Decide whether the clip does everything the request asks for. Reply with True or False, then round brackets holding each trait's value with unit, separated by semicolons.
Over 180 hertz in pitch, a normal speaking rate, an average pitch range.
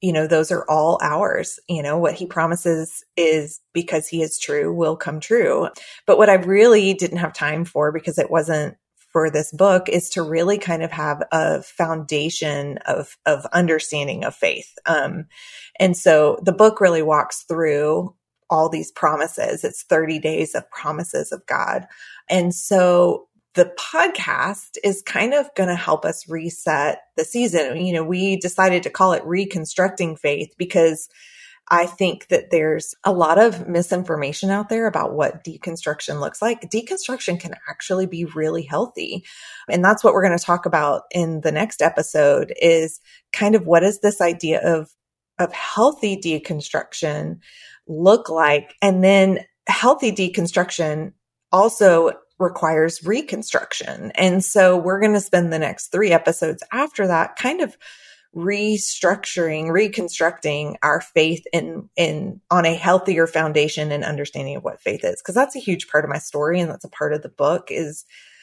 False (175 Hz; 165 wpm; 3.4 semitones)